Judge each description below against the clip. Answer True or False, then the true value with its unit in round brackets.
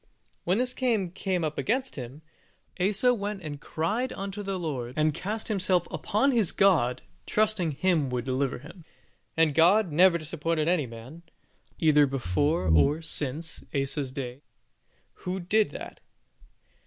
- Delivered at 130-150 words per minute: True (140 wpm)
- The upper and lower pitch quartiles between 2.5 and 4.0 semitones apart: False (5.5 semitones)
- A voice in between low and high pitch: True (165 Hz)